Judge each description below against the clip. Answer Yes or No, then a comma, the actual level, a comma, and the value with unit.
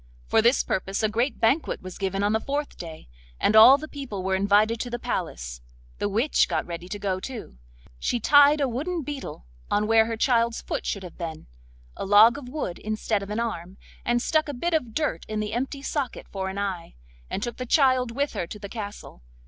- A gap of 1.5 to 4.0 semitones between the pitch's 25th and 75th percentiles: No, average, 5.0 semitones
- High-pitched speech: Yes, high, 220 Hz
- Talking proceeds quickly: Yes, fast, 220 wpm